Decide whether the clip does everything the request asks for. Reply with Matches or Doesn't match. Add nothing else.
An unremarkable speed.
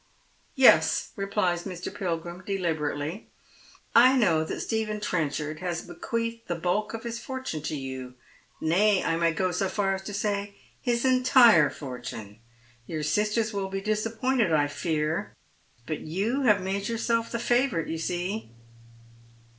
Matches